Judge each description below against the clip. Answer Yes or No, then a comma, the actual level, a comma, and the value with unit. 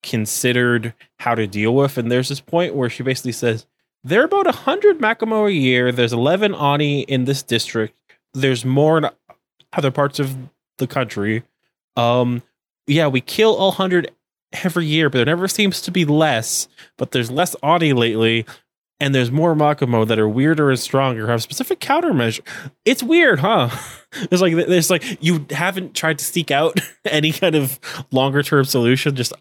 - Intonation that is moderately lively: No, wide, 5.7 semitones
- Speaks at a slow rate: No, average, 175 wpm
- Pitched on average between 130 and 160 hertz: Yes, medium, 140 Hz